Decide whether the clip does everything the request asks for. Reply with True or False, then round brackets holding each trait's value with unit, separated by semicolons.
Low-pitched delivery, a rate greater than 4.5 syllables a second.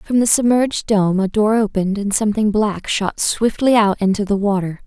False (210 Hz; 5.2 syllables/s)